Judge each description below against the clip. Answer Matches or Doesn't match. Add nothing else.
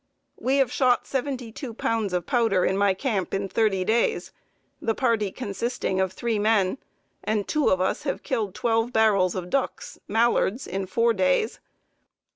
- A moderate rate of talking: Matches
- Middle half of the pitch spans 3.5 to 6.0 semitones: Matches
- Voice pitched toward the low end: Doesn't match